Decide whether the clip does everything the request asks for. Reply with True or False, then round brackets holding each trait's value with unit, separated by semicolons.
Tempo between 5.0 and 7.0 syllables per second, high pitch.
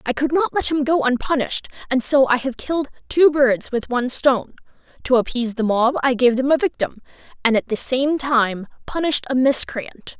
True (5.4 syllables/s; 260 Hz)